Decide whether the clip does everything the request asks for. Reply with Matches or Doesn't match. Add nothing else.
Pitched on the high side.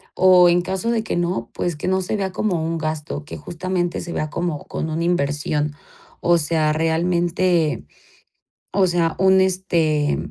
Doesn't match